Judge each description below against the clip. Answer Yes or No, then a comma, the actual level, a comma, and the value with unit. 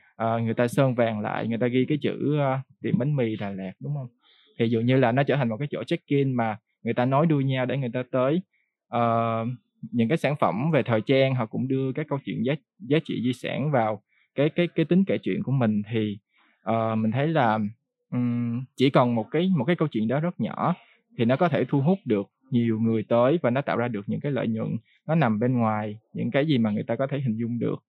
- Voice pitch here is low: Yes, low, 125 Hz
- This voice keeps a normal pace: No, fast, 255 wpm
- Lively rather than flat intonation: No, average, 4.3 semitones